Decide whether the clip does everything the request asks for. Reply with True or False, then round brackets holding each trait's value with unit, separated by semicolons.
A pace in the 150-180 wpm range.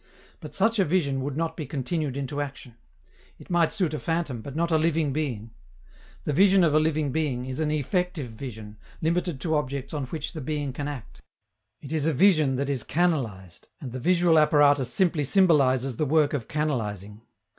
False (190 wpm)